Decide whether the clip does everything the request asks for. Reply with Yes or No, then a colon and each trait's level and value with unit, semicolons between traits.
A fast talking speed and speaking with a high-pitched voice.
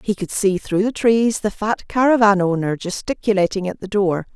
No: average, 195 wpm; high, 200 Hz